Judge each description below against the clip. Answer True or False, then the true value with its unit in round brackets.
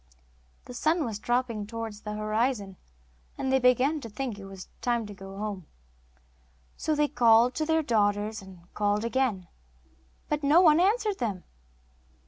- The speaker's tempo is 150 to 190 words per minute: True (155 wpm)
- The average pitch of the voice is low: False (230 Hz)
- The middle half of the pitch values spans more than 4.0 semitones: True (4.6 semitones)